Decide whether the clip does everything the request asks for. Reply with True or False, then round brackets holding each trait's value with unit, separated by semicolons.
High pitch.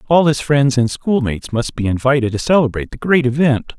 False (130 Hz)